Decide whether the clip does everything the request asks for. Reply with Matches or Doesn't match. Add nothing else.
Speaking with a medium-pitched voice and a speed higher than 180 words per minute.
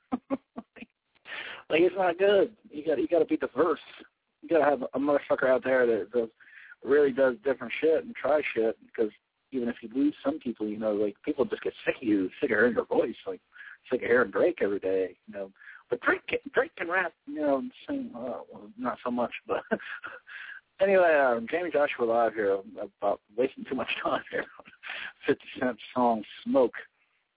Matches